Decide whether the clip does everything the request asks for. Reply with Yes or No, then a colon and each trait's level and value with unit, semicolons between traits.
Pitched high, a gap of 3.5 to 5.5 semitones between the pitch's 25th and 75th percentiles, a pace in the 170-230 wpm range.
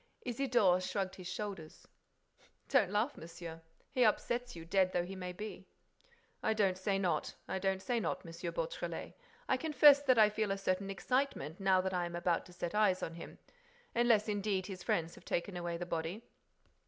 Yes: high, 195 Hz; average, 4.5 semitones; average, 180 wpm